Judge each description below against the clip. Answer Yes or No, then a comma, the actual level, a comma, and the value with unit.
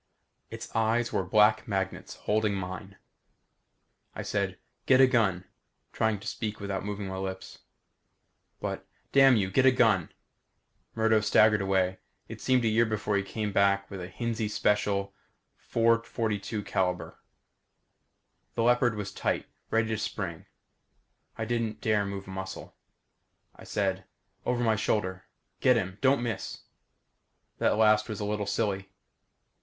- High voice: No, low, 105 Hz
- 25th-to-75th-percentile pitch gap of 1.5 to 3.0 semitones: Yes, narrow, 2.6 semitones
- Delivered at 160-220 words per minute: No, average, 140 wpm